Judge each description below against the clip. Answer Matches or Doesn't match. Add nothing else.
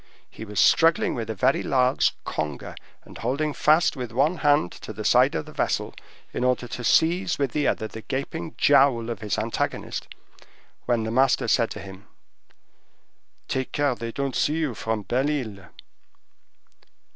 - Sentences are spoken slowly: Doesn't match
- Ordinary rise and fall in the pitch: Matches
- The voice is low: Matches